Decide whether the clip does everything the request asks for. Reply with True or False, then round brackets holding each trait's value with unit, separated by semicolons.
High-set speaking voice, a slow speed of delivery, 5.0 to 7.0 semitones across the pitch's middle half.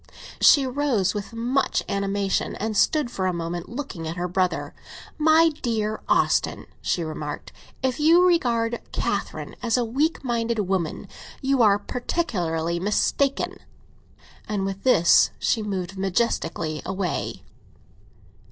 True (210 Hz; 125 wpm; 5.6 semitones)